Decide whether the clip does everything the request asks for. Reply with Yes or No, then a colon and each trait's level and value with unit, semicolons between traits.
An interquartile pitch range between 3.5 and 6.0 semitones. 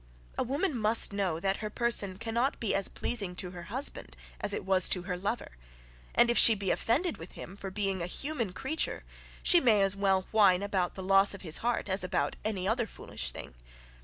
Yes: average, 3.9 semitones